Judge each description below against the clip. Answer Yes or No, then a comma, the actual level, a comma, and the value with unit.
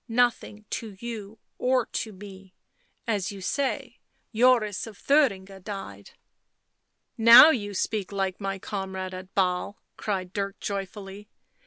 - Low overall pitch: No, high, 200 Hz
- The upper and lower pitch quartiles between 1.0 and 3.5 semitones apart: Yes, narrow, 2.6 semitones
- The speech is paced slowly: Yes, slow, 130 wpm